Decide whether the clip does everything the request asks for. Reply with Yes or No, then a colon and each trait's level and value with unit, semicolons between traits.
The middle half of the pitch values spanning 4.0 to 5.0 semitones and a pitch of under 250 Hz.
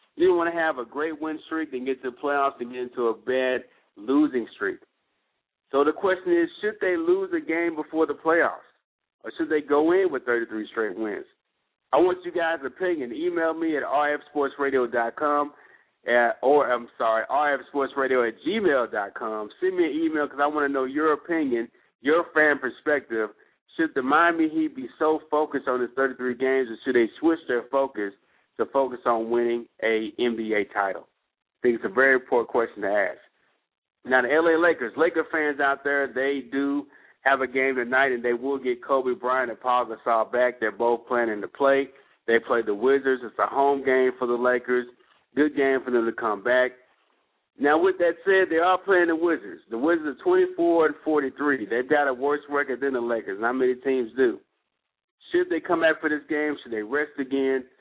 Yes: average, 4.4 semitones; medium, 140 Hz